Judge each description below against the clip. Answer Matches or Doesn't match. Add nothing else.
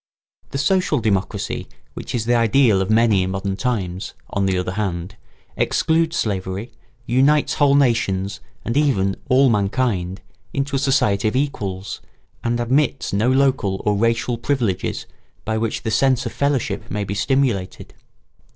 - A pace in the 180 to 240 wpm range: Doesn't match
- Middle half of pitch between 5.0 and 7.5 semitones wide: Matches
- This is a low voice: Matches